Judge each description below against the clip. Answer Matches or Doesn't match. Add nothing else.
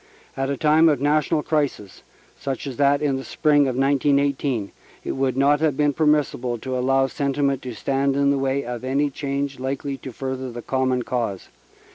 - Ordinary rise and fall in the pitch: Doesn't match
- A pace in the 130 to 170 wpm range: Doesn't match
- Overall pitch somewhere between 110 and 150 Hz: Matches